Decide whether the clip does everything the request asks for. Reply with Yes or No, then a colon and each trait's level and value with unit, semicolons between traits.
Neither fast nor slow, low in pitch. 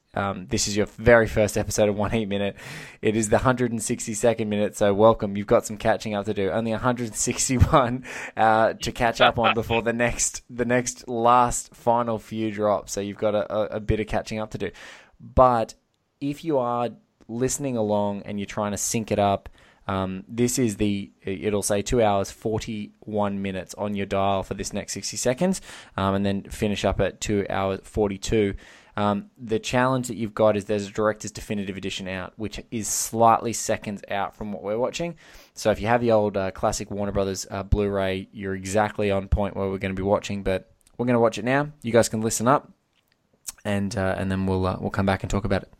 No: fast, 230 wpm; low, 105 Hz